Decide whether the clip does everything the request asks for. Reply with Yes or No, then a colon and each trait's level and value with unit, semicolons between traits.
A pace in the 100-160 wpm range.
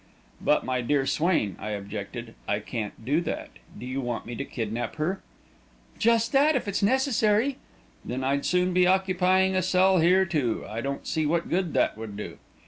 No: average, 185 wpm